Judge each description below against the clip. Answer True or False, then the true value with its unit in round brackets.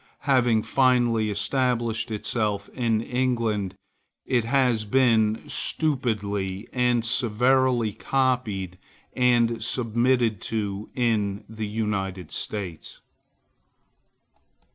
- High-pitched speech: False (115 Hz)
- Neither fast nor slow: False (80 wpm)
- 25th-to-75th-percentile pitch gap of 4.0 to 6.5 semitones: False (2.9 semitones)